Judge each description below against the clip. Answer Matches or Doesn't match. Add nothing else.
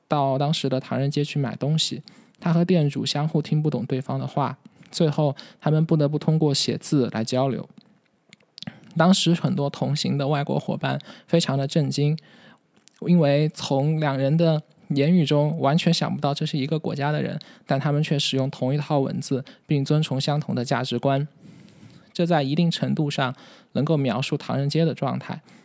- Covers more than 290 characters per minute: Doesn't match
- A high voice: Doesn't match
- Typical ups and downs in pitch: Matches